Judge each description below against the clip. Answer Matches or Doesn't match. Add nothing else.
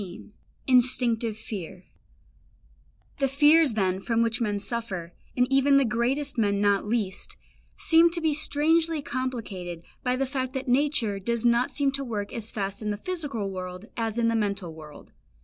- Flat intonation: Doesn't match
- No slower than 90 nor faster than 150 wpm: Doesn't match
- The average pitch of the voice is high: Matches